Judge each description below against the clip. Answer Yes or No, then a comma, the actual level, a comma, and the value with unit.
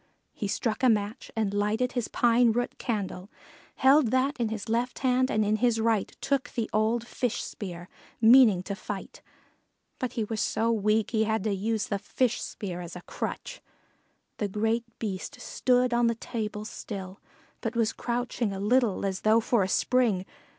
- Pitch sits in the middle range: No, high, 225 Hz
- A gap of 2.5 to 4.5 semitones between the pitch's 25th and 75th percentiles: Yes, average, 2.9 semitones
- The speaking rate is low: No, average, 180 wpm